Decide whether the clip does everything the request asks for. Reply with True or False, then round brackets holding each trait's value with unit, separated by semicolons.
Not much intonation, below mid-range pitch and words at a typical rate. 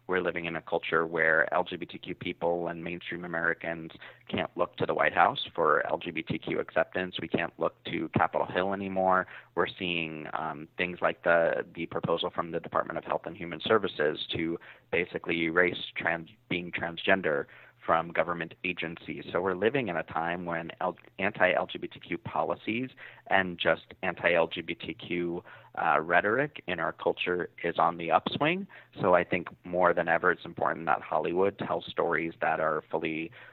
True (1.4 semitones; 85 Hz; 165 wpm)